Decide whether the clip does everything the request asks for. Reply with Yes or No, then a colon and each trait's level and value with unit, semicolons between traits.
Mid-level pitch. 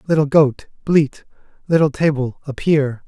Yes: medium, 145 Hz